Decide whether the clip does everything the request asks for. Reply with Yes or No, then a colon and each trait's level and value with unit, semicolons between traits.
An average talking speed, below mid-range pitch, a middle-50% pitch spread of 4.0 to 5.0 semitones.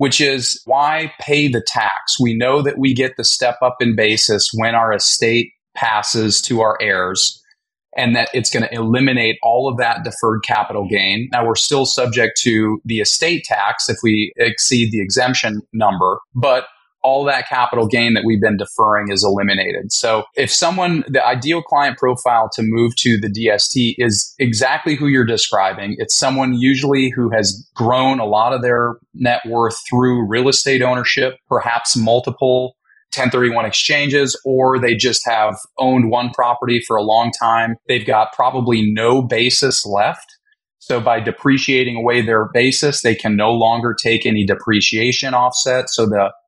No: average, 170 wpm; low, 120 Hz; average, 2.7 semitones